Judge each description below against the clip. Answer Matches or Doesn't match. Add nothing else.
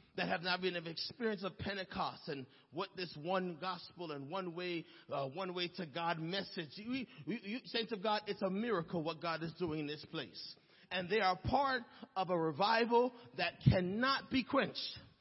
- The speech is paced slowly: Doesn't match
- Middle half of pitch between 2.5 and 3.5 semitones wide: Doesn't match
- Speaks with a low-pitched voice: Doesn't match